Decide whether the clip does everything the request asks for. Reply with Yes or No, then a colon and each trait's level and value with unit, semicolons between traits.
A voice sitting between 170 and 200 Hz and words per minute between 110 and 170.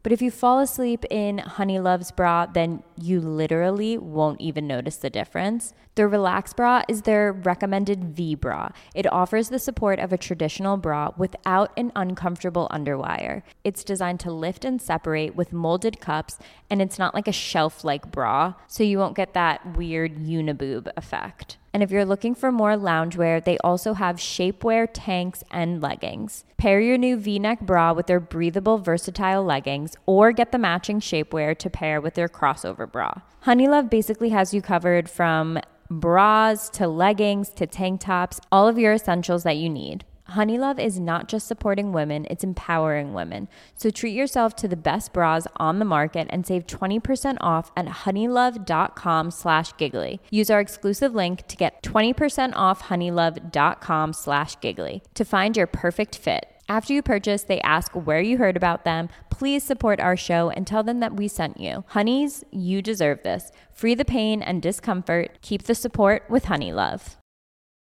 Yes: medium, 185 Hz; average, 165 wpm